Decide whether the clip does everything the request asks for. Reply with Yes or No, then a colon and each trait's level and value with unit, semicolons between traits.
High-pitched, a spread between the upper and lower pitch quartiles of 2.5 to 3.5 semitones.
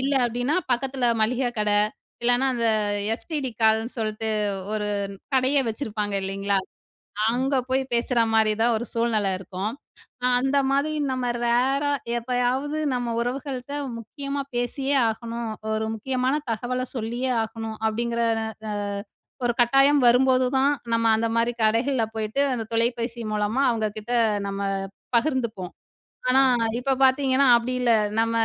Yes: high, 240 Hz; average, 2.8 semitones